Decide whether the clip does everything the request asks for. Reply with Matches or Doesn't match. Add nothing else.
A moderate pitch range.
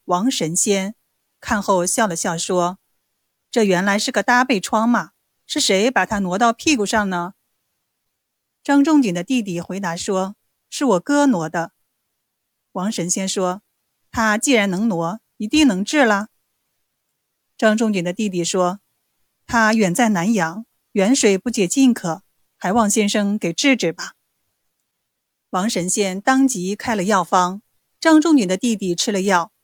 Matches